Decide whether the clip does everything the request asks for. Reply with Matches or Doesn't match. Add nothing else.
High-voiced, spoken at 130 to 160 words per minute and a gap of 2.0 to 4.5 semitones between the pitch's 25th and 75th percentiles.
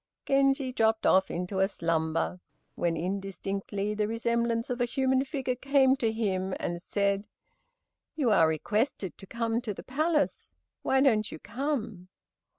Doesn't match